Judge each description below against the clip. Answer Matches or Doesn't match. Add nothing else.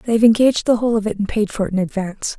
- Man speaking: Doesn't match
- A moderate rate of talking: Doesn't match